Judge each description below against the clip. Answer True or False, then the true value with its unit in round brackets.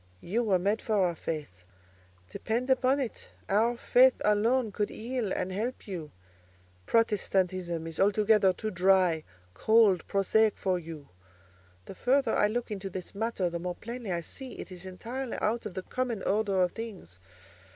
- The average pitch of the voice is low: False (200 Hz)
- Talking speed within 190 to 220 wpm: False (160 wpm)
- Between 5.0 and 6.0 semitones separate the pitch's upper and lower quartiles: False (4.2 semitones)